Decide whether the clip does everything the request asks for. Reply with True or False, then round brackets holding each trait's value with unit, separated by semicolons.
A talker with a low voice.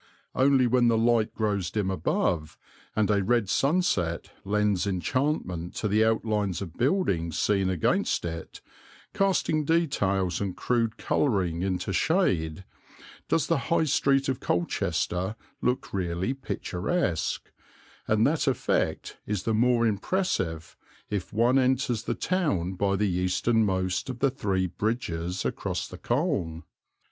True (105 Hz)